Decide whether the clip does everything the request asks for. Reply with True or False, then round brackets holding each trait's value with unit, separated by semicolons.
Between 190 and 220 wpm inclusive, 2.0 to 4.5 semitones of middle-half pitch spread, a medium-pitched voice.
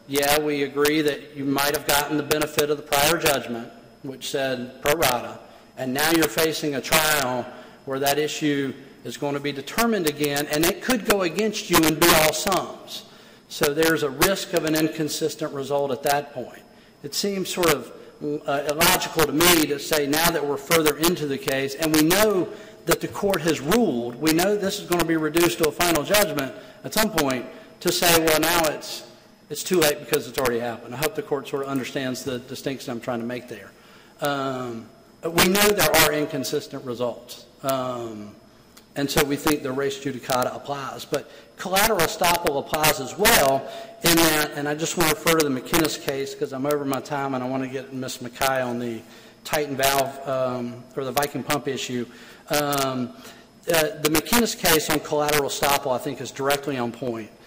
True (200 wpm; 3.3 semitones; 145 Hz)